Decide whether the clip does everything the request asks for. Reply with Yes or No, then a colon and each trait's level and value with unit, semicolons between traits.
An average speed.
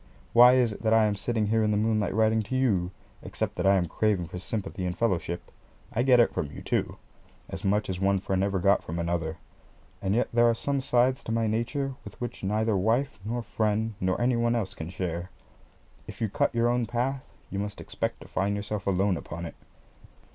No: fast, 220 wpm